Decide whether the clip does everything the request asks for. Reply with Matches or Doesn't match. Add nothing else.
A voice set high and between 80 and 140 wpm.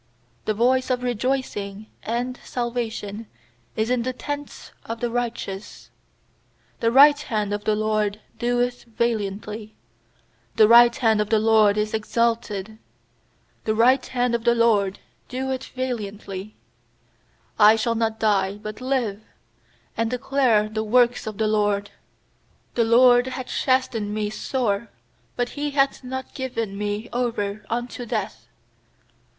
Matches